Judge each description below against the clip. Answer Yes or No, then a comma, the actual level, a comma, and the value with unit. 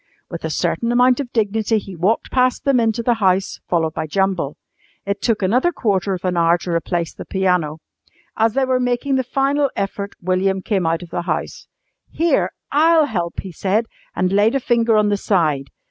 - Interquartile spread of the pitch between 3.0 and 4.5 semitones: No, average, 5.1 semitones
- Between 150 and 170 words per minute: No, average, 195 wpm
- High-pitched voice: Yes, high, 200 Hz